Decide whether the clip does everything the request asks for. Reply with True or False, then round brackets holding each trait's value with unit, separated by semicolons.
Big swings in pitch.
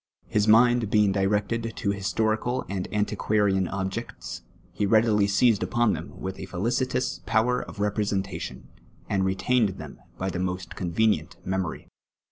False (2.7 semitones)